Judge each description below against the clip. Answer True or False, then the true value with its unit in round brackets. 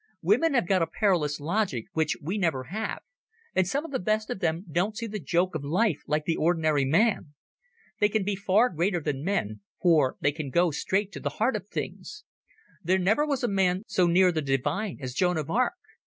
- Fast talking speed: True (215 wpm)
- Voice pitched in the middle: True (180 Hz)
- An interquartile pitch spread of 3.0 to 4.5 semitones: False (5.2 semitones)